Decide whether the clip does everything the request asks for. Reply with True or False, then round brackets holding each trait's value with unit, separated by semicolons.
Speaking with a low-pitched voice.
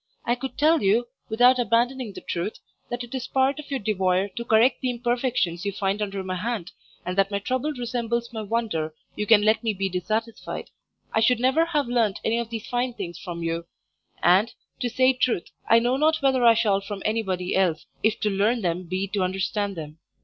False (220 Hz)